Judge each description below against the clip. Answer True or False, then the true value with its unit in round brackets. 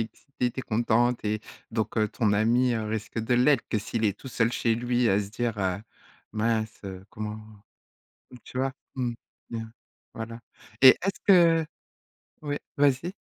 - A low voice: True (115 Hz)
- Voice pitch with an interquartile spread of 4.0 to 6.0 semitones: False (2.7 semitones)